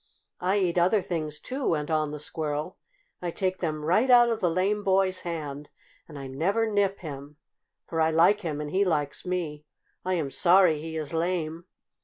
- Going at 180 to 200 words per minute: Yes, average, 190 wpm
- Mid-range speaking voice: Yes, medium, 170 Hz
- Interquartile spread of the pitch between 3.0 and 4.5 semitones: Yes, average, 3.7 semitones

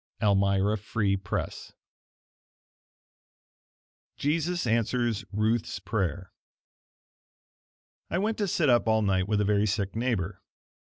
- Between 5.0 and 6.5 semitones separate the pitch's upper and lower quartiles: No, average, 3.3 semitones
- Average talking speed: No, slow, 105 wpm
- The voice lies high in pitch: No, low, 110 Hz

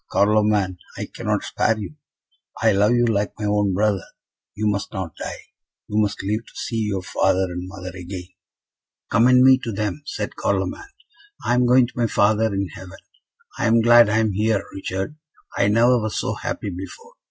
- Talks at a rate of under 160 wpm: No, average, 185 wpm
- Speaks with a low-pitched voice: Yes, low, 105 Hz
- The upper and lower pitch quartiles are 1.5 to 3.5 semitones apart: Yes, average, 2.9 semitones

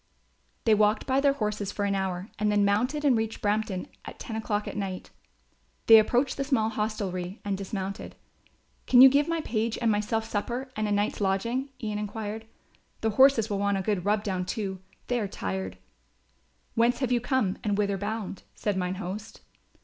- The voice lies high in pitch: Yes, high, 210 Hz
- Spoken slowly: No, average, 190 wpm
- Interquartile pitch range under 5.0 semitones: Yes, average, 2.7 semitones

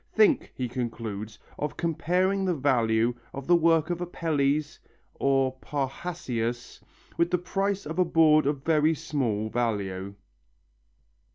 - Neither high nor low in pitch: Yes, medium, 145 Hz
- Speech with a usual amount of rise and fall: No, wide, 5.8 semitones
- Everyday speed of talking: No, slow, 125 wpm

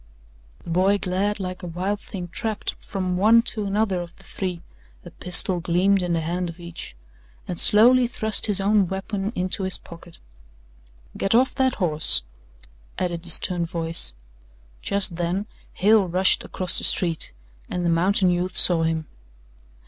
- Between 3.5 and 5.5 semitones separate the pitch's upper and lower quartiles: No, average, 2.7 semitones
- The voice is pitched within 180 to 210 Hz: Yes, medium, 185 Hz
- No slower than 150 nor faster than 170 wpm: Yes, average, 160 wpm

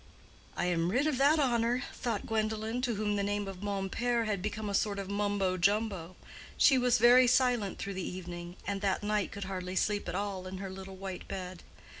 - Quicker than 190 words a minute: Yes, fast, 205 wpm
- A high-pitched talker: Yes, high, 205 Hz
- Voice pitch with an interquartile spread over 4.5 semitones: No, average, 3.2 semitones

